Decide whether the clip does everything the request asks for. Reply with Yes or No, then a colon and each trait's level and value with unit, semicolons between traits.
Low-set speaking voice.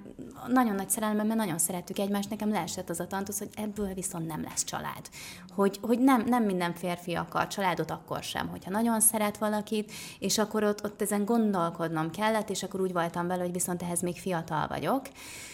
No: high, 200 Hz